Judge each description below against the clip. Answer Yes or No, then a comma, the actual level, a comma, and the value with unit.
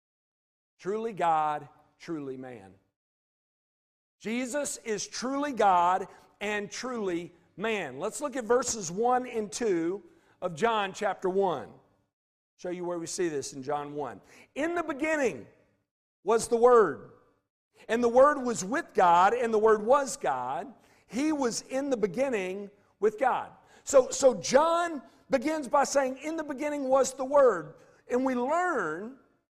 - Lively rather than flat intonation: Yes, wide, 7.7 semitones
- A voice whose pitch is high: Yes, high, 230 Hz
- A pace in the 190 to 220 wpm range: No, average, 145 wpm